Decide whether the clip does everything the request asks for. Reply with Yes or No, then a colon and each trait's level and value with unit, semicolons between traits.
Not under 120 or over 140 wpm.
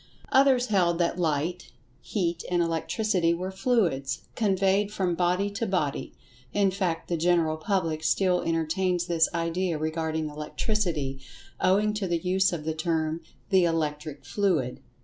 Yes: slow, 135 wpm